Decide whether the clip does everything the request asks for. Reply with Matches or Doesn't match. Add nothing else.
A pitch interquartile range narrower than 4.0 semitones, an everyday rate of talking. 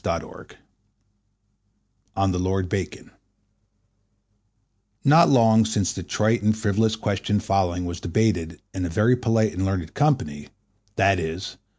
Doesn't match